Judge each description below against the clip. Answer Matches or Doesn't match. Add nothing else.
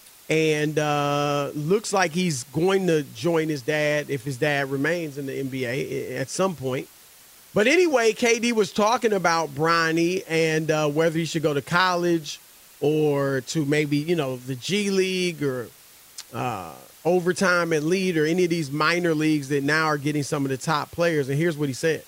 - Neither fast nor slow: Matches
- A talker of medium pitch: Matches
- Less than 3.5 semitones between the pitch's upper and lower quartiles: Matches